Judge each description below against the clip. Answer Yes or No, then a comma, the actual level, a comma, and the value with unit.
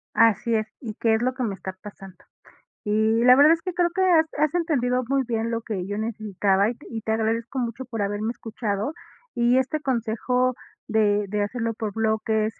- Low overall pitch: No, high, 225 Hz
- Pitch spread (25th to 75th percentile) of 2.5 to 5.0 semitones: Yes, average, 2.9 semitones